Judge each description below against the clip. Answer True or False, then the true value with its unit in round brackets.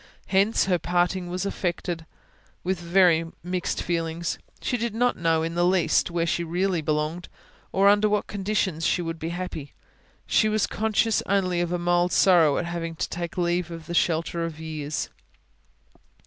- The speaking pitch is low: False (175 Hz)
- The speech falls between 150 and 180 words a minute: True (170 wpm)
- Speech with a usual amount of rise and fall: False (2.3 semitones)